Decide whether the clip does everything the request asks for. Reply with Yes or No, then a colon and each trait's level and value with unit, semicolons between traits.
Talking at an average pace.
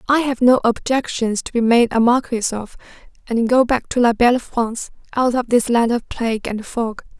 No: fast, 210 wpm